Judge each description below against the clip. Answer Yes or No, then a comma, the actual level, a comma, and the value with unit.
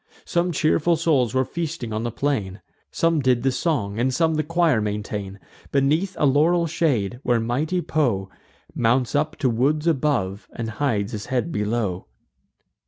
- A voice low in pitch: Yes, low, 130 Hz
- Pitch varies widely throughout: Yes, wide, 5.8 semitones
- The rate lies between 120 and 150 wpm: No, average, 160 wpm